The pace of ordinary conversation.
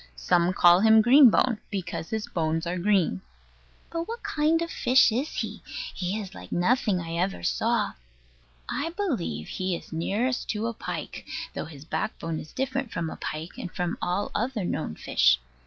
Yes: average, 175 wpm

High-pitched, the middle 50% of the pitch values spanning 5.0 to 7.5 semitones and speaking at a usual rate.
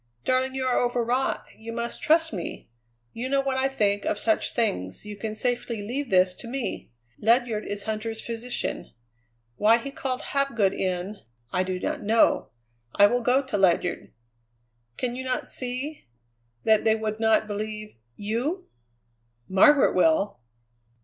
No: high, 230 Hz; average, 3.7 semitones; average, 150 wpm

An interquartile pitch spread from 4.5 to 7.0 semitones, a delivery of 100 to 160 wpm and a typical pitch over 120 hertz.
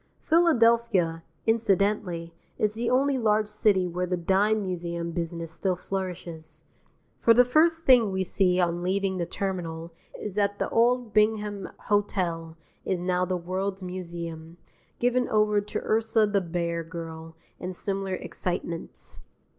No: average, 3.8 semitones; average, 140 wpm; high, 190 Hz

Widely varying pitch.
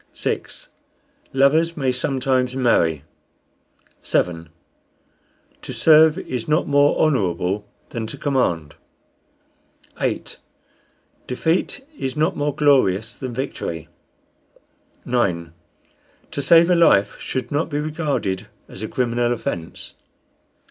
Yes: wide, 6.6 semitones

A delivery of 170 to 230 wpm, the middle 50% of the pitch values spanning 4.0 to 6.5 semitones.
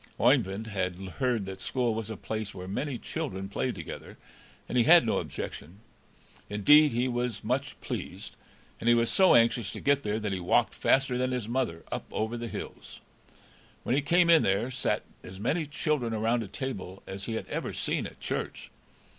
Yes: average, 190 wpm; average, 4.6 semitones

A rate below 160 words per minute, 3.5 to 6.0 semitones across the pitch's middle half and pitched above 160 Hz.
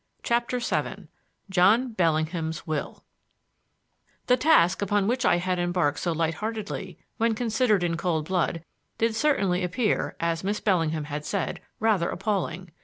Yes: average, 140 wpm; average, 4.8 semitones; medium, 185 Hz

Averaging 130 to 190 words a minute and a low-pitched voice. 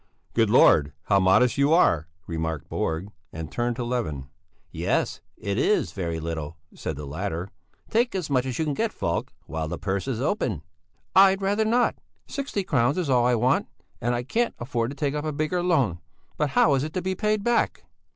No: average, 200 wpm; low, 125 Hz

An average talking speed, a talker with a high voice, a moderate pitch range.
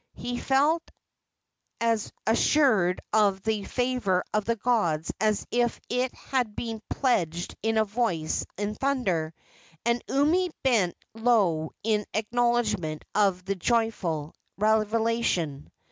No: slow, 115 wpm; high, 220 Hz; average, 4.3 semitones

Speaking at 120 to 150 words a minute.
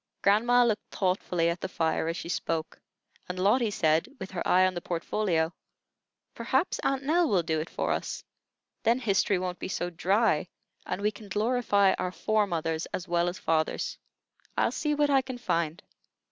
No: average, 180 wpm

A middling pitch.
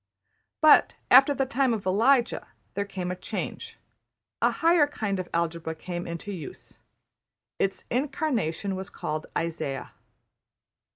No: high, 195 Hz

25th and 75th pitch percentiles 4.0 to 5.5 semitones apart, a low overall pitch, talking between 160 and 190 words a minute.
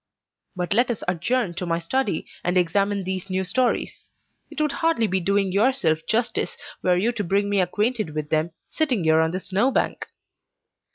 No: average, 4.8 semitones; high, 195 Hz; average, 180 wpm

